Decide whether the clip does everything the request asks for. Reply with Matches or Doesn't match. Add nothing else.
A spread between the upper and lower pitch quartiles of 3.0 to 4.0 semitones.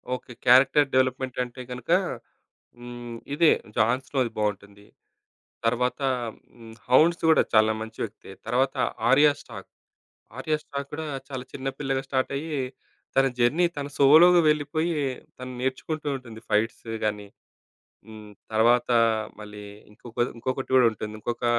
Matches